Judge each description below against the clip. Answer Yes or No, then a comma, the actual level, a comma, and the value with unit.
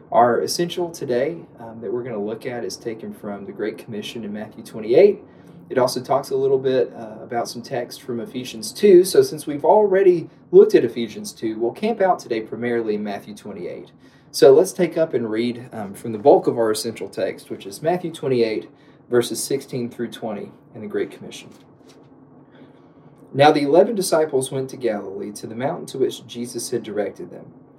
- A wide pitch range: Yes, wide, 7.3 semitones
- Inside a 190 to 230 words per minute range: Yes, average, 195 wpm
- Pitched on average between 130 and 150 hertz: Yes, low, 135 Hz